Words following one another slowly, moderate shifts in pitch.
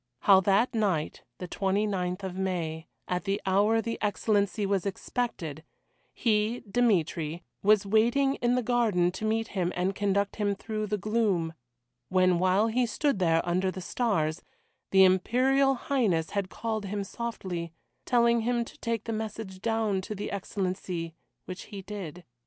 No: average, 155 wpm; average, 3.4 semitones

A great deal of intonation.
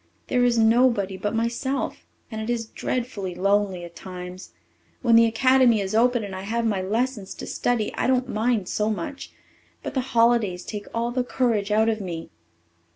No: average, 3.4 semitones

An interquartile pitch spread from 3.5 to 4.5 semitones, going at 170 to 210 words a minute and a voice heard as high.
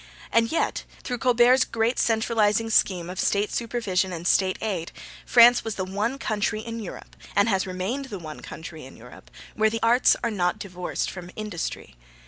Yes: average, 4.0 semitones; average, 175 wpm; high, 210 Hz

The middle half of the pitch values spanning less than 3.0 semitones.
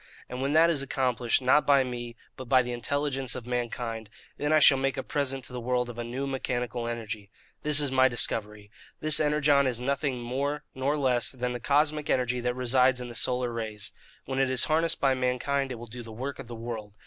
Yes: narrow, 2.5 semitones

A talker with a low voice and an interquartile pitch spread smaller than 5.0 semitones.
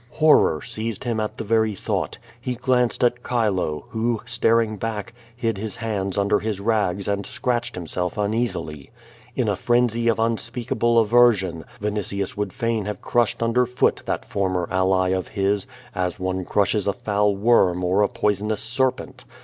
Yes: low, 105 Hz; average, 3.2 semitones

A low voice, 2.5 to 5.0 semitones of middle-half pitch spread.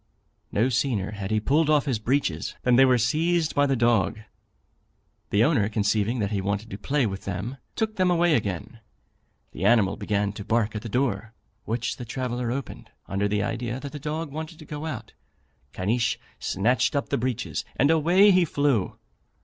No: low, 120 Hz; wide, 5.5 semitones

